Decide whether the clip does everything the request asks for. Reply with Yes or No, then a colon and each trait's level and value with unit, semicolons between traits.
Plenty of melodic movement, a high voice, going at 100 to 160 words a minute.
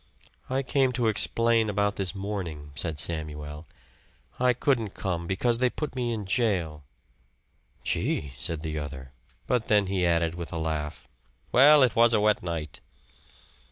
No: wide, 6.5 semitones; very low, 95 Hz; average, 155 wpm